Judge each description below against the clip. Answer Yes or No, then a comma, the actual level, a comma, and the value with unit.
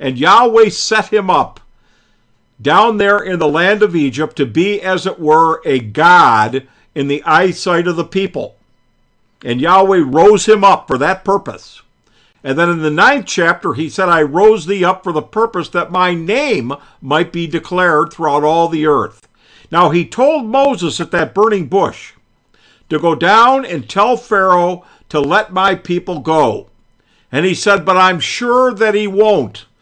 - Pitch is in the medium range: Yes, medium, 175 Hz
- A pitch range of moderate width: Yes, average, 4.6 semitones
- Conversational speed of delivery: Yes, average, 175 wpm